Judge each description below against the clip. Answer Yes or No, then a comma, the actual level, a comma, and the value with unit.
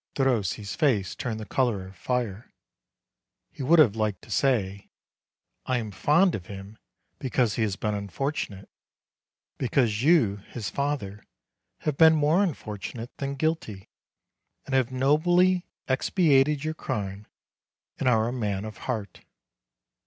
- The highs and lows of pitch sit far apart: Yes, wide, 5.7 semitones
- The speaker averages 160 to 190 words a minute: No, slow, 135 wpm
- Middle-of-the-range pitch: No, low, 125 Hz